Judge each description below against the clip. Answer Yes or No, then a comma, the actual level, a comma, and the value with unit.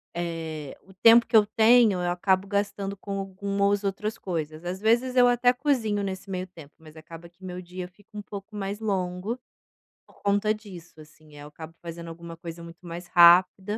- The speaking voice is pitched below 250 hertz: Yes, high, 190 Hz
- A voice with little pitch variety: No, average, 3.3 semitones